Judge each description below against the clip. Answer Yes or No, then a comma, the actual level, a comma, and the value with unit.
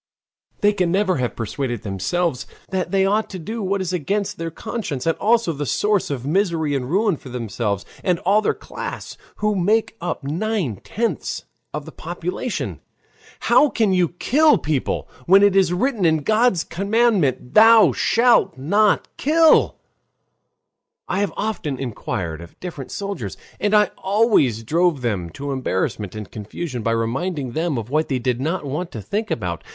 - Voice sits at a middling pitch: Yes, medium, 175 Hz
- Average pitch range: No, wide, 7.9 semitones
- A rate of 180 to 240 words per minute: No, average, 165 wpm